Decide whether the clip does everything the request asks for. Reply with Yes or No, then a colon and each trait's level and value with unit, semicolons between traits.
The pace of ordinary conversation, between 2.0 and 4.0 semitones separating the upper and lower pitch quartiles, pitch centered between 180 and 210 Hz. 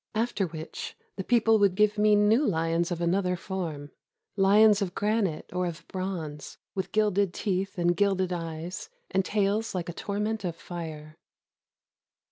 Yes: average, 160 wpm; average, 3.3 semitones; high, 190 Hz